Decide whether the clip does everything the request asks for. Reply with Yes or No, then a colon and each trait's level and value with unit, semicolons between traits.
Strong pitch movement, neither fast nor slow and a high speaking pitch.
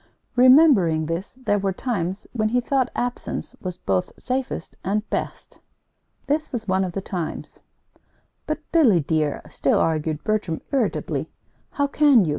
Yes: wide, 7.2 semitones; average, 145 wpm; high, 210 Hz